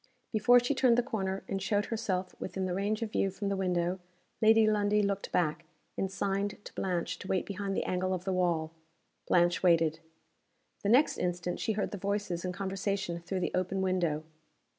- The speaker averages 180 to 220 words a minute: Yes, average, 190 wpm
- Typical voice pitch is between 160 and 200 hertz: Yes, high, 190 Hz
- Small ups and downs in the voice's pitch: Yes, narrow, 2.2 semitones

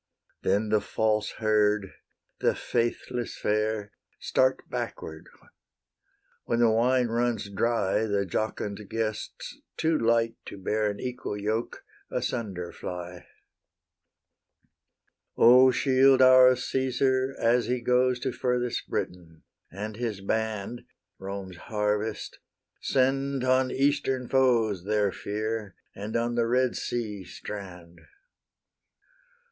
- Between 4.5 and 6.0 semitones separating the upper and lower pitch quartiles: No, average, 3.4 semitones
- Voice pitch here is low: Yes, low, 115 Hz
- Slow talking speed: Yes, slow, 110 wpm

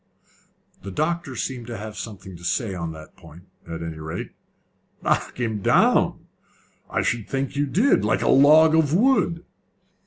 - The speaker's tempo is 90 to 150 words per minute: No, average, 160 wpm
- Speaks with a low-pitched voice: Yes, low, 115 Hz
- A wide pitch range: Yes, wide, 8.2 semitones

